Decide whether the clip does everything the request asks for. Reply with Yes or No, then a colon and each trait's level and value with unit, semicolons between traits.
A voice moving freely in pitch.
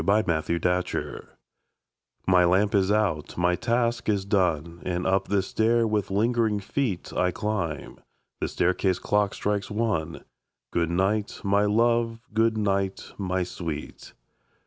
No: average, 3.2 semitones